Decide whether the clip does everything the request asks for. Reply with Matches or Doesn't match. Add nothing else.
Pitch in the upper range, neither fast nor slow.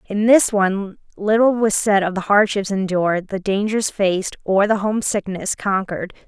Matches